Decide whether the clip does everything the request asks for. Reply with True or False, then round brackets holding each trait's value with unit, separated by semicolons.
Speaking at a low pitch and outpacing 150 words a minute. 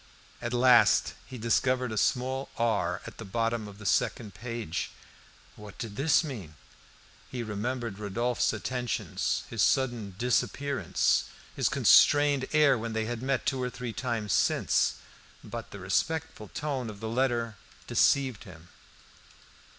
False (120 Hz; 140 wpm)